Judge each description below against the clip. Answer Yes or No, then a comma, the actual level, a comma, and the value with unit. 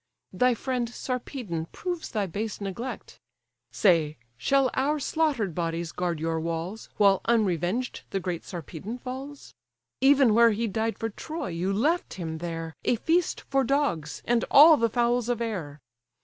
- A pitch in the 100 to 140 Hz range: No, high, 225 Hz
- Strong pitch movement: Yes, wide, 6.9 semitones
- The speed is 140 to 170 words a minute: Yes, average, 150 wpm